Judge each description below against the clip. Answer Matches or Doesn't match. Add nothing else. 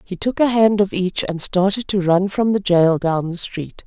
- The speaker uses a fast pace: Matches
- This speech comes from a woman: Matches